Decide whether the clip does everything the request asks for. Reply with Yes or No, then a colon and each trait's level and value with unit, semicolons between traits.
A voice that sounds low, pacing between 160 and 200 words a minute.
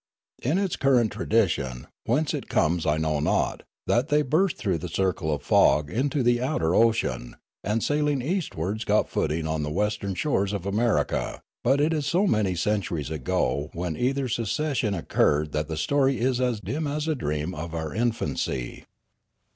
Yes: low, 105 Hz; average, 175 wpm